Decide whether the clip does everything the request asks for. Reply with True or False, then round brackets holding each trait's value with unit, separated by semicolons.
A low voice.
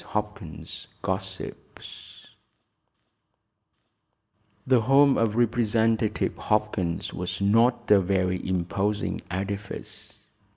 True (105 Hz)